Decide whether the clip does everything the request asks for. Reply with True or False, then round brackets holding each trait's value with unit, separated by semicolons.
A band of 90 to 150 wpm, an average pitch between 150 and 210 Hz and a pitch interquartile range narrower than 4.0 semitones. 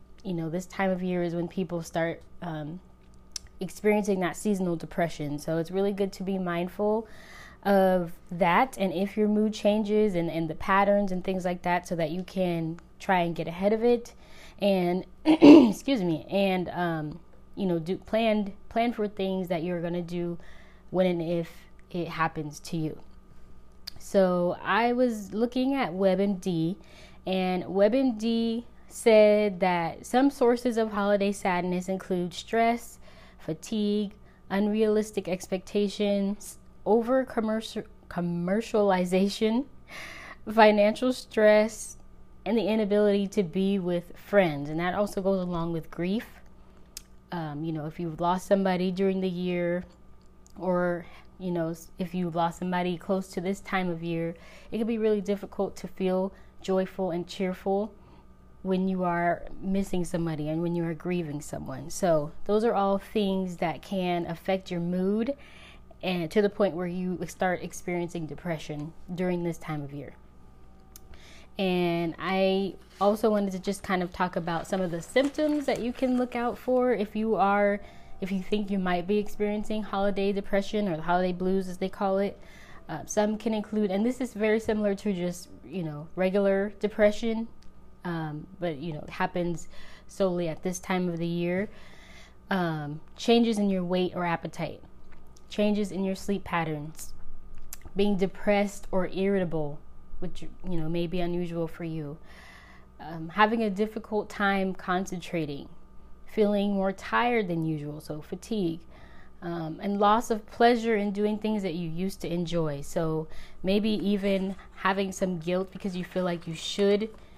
False (160 wpm; 185 Hz; 3.2 semitones)